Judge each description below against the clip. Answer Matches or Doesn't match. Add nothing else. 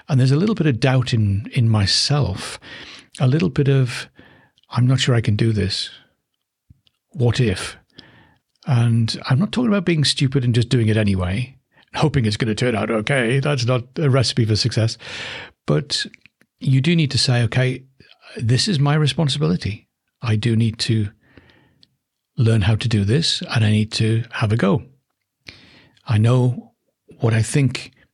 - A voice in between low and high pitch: Doesn't match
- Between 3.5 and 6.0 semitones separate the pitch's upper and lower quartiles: Matches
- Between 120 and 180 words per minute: Matches